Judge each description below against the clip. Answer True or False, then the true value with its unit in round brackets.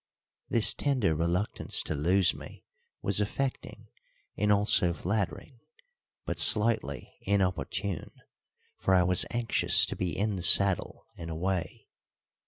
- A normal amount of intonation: True (3.3 semitones)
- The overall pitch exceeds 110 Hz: False (95 Hz)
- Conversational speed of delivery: False (120 wpm)